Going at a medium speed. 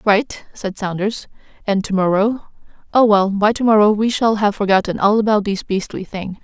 Yes: average, 175 wpm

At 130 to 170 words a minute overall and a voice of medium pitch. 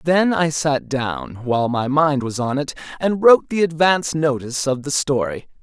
No: average, 190 wpm; medium, 145 Hz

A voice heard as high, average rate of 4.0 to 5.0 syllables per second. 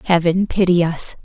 No: medium, 175 Hz; 4.7 syllables/s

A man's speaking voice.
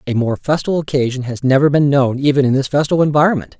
Yes: male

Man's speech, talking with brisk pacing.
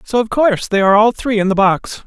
Yes: male; fast, 290 wpm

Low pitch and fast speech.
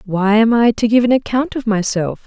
No: high, 225 Hz; fast, 240 wpm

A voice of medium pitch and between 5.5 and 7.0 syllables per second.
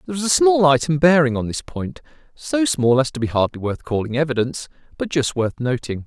Yes: medium, 145 Hz; 5.8 syllables/s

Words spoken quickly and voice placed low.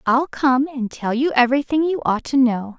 No: fast, 215 wpm; very high, 265 Hz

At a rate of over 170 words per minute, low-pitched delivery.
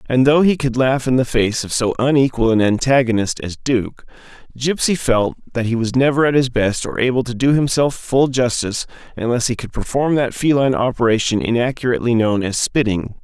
Yes: average, 190 wpm; low, 125 Hz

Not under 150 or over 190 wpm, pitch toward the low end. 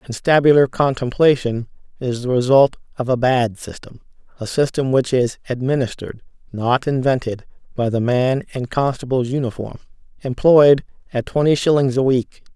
No: slow, 135 wpm; low, 130 Hz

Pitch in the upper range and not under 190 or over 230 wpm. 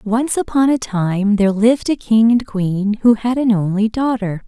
Yes: high, 220 Hz; average, 200 wpm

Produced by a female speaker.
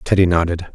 No: male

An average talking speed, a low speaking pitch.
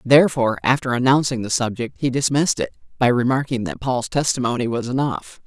Yes: average, 165 wpm; low, 130 Hz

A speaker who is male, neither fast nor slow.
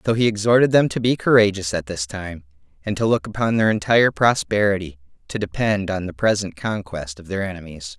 Yes: male; average, 195 wpm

